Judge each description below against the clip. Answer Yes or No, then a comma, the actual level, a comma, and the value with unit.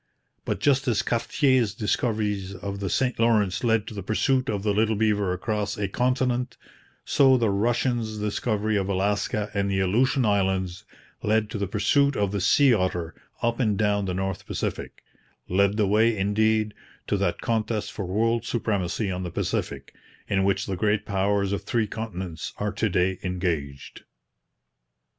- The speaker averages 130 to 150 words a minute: No, average, 165 wpm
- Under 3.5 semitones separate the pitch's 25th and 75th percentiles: Yes, average, 2.7 semitones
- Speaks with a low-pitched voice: Yes, low, 105 Hz